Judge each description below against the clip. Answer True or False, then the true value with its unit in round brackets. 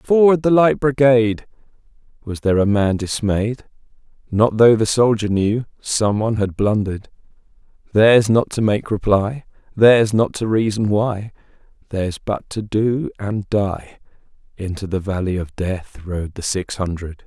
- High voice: False (105 Hz)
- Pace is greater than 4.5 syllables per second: False (4.3 syllables/s)